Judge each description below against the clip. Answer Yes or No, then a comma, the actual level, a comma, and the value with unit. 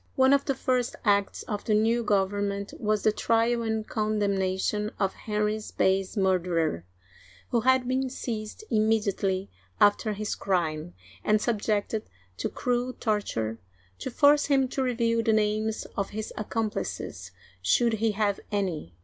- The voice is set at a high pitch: Yes, high, 215 Hz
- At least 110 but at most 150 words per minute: Yes, average, 145 wpm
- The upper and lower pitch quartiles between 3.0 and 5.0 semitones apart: No, narrow, 2.5 semitones